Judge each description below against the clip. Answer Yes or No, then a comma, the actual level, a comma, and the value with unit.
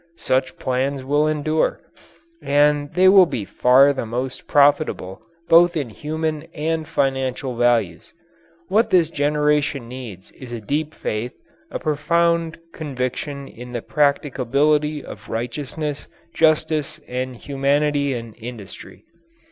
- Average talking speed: No, slow, 120 wpm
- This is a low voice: No, medium, 145 Hz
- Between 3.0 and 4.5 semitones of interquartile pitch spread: Yes, average, 3.4 semitones